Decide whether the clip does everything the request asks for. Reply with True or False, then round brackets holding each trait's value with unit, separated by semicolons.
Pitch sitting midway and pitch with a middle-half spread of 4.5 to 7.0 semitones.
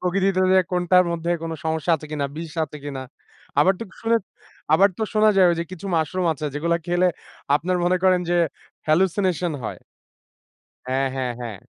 False (170 Hz; 3.1 semitones)